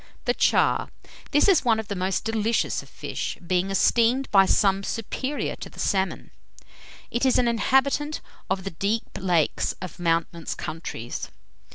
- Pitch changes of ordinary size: Yes, average, 4.5 semitones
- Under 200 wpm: Yes, average, 155 wpm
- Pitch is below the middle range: No, high, 200 Hz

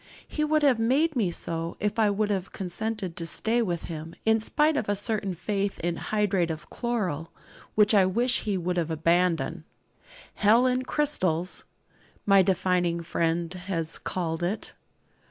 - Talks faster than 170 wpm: No, average, 155 wpm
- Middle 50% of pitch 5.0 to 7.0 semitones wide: No, average, 4.5 semitones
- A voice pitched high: Yes, high, 195 Hz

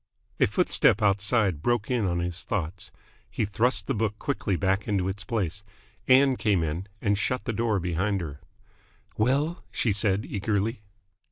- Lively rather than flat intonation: No, average, 3.2 semitones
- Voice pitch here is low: Yes, low, 105 Hz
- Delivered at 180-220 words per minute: No, average, 160 wpm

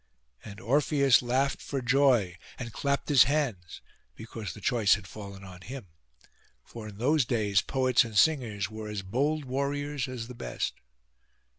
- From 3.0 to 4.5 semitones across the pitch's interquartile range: No, average, 5.0 semitones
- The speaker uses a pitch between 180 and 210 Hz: No, low, 120 Hz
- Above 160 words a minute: No, average, 155 wpm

